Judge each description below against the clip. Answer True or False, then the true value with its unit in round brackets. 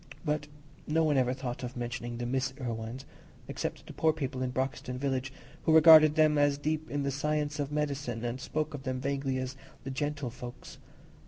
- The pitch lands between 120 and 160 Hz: True (135 Hz)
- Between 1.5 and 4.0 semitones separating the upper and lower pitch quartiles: True (2.8 semitones)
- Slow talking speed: False (185 wpm)